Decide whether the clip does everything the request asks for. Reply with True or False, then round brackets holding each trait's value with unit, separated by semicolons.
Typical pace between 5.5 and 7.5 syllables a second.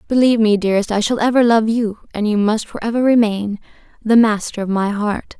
True (5.7 syllables/s)